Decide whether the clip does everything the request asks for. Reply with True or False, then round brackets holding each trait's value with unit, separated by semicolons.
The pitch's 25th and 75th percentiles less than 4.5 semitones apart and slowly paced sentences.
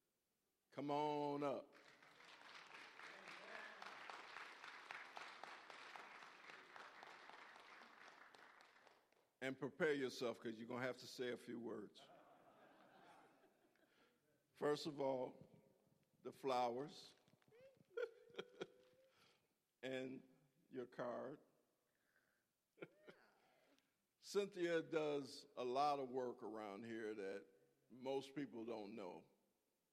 True (3.3 semitones; 75 wpm)